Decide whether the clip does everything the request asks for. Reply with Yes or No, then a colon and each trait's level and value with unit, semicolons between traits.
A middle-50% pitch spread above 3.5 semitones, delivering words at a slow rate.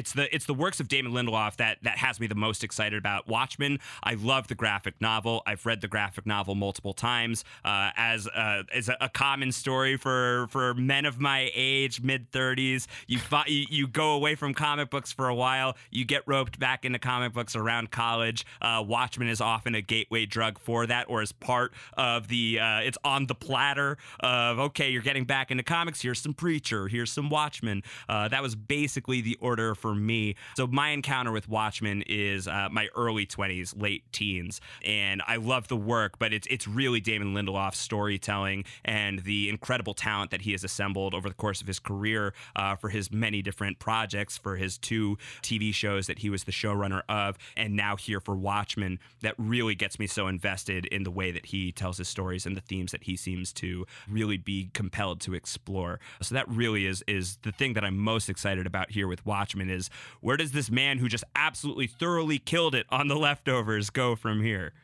No: average, 4.2 semitones; fast, 205 wpm